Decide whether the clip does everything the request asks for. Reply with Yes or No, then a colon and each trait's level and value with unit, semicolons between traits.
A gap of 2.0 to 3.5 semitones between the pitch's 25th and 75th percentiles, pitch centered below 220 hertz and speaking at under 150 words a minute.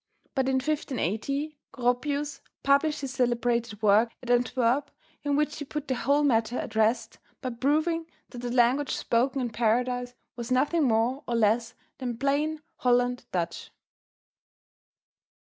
No: average, 3.2 semitones; very high, 250 Hz; average, 140 wpm